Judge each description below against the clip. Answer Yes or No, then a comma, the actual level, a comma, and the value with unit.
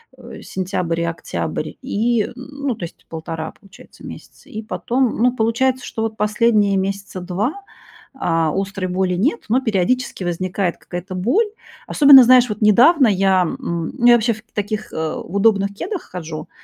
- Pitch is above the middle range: Yes, high, 205 Hz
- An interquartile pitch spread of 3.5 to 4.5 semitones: No, average, 4.9 semitones